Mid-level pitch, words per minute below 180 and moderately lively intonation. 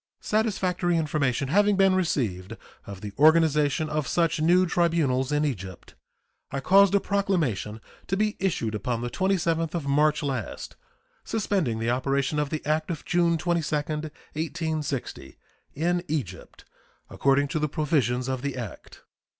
Yes: medium, 155 Hz; average, 140 wpm; average, 4.7 semitones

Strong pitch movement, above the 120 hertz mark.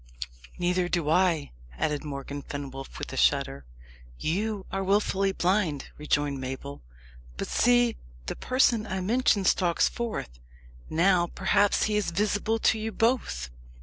Yes: wide, 6.5 semitones; medium, 185 Hz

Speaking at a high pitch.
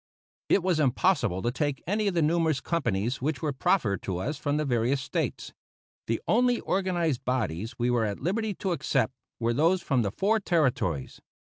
No: medium, 145 Hz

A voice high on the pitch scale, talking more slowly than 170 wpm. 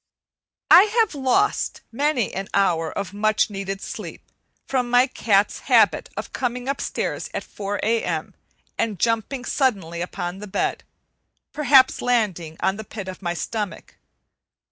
Yes: high, 215 Hz; average, 140 wpm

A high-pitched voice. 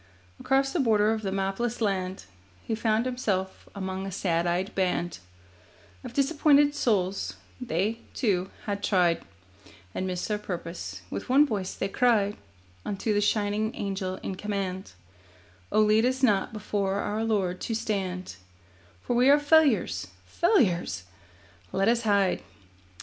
Yes: high, 205 Hz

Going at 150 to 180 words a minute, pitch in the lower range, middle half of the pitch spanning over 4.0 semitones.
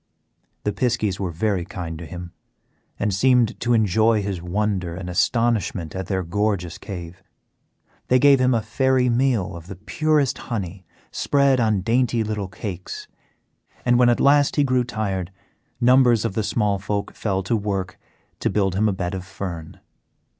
Yes: average, 165 wpm; low, 105 Hz; average, 4.4 semitones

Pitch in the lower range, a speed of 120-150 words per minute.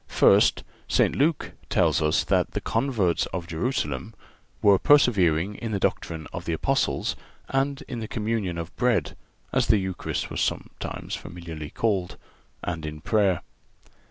Yes: very low, 95 Hz; average, 140 wpm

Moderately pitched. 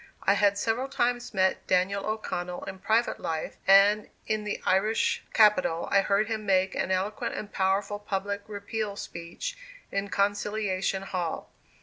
No: high, 200 Hz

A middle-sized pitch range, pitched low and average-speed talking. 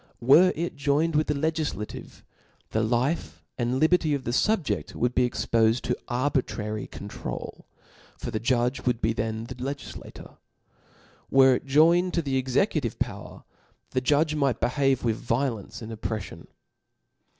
Yes: average, 4.2 semitones; low, 130 Hz; average, 150 wpm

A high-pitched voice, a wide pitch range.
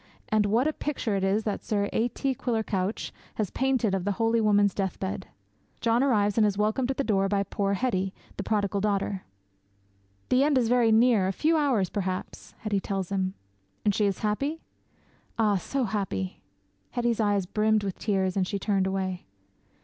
No: high, 205 Hz; average, 3.0 semitones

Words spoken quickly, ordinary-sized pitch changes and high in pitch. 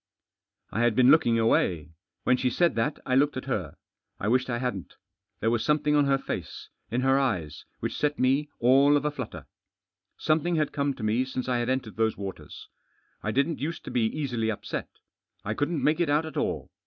No: fast, 215 wpm; average, 4.4 semitones; low, 130 Hz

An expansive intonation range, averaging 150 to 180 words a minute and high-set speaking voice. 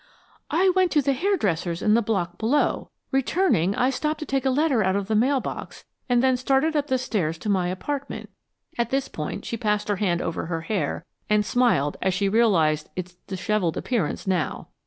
No: wide, 6.5 semitones; average, 200 wpm; high, 220 Hz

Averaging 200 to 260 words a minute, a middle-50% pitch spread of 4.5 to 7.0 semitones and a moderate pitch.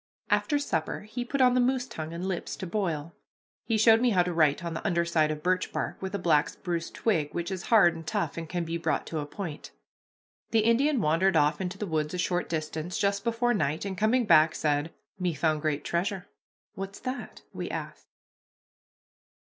Yes: fast, 205 wpm; average, 5.0 semitones; medium, 180 Hz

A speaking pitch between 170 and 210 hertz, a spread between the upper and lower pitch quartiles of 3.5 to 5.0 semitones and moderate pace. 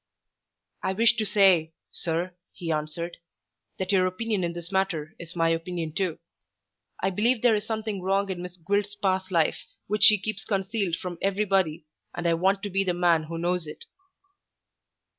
No: medium, 185 Hz; average, 2.9 semitones; average, 175 wpm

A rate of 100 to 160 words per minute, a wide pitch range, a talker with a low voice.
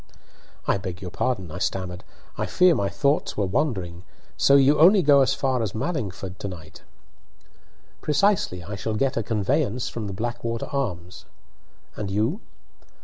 Yes: average, 155 wpm; wide, 6.6 semitones; low, 110 Hz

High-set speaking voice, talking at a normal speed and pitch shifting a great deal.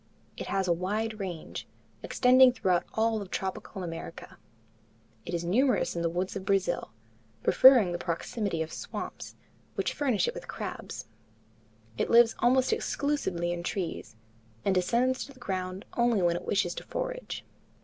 Yes: high, 195 Hz; average, 155 wpm; wide, 5.9 semitones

